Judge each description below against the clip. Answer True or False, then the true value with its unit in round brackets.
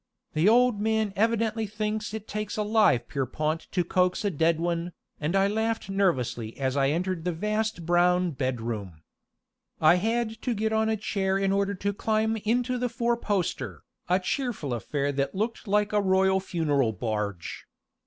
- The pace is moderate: True (170 wpm)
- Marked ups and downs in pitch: True (5.8 semitones)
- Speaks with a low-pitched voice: False (195 Hz)